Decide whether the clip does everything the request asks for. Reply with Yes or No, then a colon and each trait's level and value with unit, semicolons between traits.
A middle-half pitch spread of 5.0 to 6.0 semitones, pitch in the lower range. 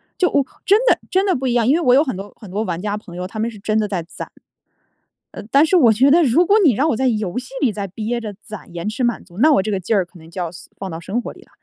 No: wide, 5.4 semitones; high, 220 Hz